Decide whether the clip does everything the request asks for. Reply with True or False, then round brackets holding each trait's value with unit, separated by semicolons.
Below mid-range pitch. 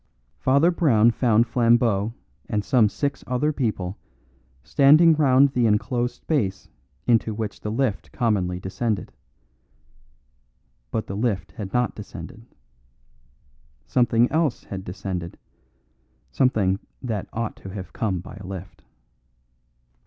True (115 Hz)